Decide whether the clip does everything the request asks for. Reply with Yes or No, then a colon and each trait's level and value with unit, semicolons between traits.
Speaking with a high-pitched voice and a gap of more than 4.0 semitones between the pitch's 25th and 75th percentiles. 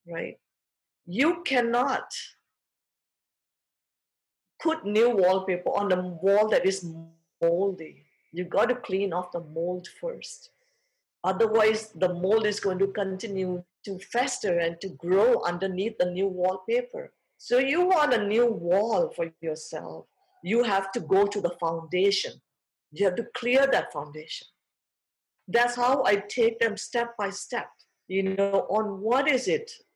Yes: high, 200 Hz; average, 5.2 semitones